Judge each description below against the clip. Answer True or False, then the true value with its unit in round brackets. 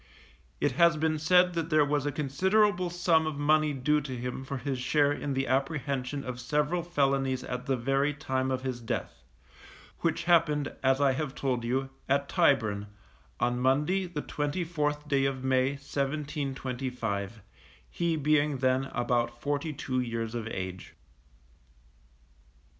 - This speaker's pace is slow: False (150 wpm)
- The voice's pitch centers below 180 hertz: True (140 Hz)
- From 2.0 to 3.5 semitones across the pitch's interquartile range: True (2.8 semitones)